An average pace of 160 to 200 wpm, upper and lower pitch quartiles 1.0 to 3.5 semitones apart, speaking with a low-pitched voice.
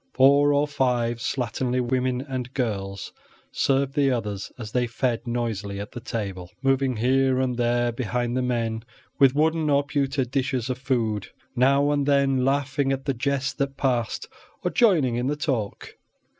Yes: average, 165 wpm; narrow, 2.5 semitones; low, 130 Hz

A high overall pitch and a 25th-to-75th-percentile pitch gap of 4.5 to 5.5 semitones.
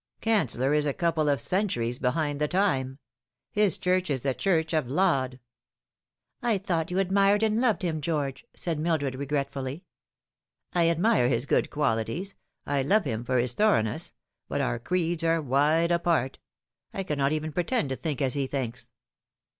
No: medium, 155 Hz; average, 5.2 semitones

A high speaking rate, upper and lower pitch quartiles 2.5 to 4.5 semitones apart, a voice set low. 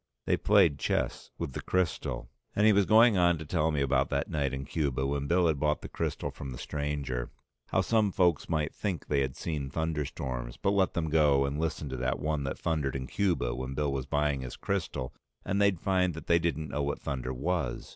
Yes: fast, 220 wpm; average, 4.2 semitones; very low, 75 Hz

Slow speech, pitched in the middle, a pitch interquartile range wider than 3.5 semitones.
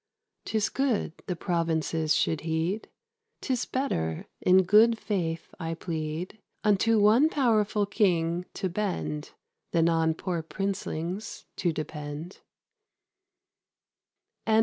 Yes: slow, 105 wpm; medium, 180 Hz; average, 4.5 semitones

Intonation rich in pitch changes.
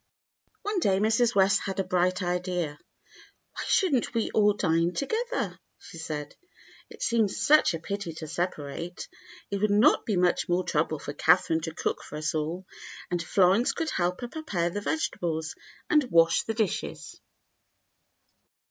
No: average, 4.8 semitones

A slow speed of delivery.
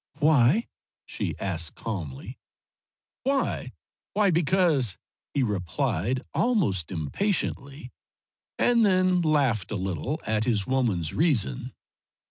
Yes: slow, 100 wpm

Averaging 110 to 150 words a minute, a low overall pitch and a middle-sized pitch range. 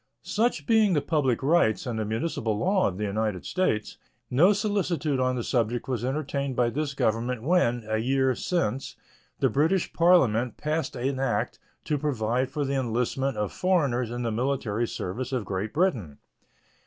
No: average, 165 wpm; low, 130 Hz; average, 5.0 semitones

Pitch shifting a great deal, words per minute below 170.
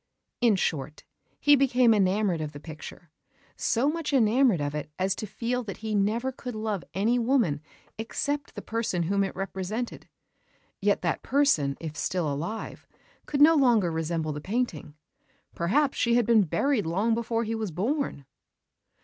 Yes: wide, 6.4 semitones; average, 160 wpm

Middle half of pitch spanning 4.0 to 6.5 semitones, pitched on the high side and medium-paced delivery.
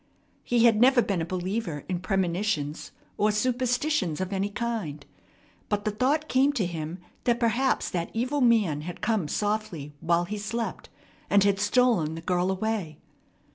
Yes: average, 5.2 semitones; high, 205 Hz; average, 160 wpm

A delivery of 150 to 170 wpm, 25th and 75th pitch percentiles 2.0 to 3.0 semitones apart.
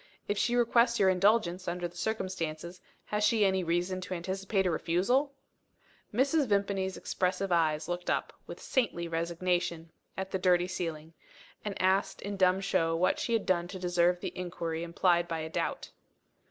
Yes: average, 165 wpm; narrow, 2.4 semitones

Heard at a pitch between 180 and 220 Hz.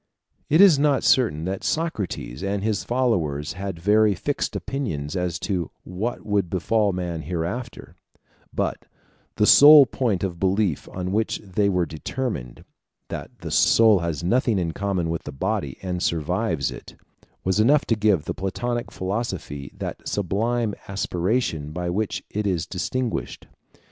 No: very low, 95 Hz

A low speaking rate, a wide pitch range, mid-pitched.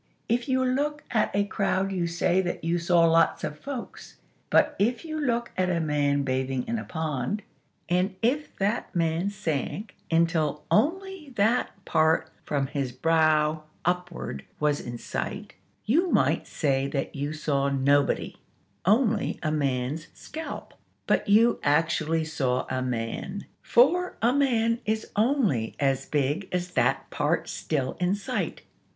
No: average, 145 wpm; wide, 7.4 semitones; medium, 170 Hz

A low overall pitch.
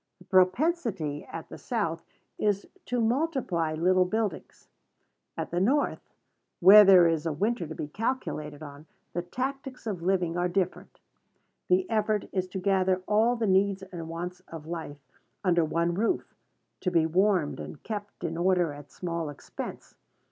No: medium, 185 Hz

